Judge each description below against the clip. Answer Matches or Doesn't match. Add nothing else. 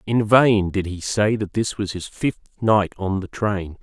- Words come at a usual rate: Doesn't match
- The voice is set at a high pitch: Doesn't match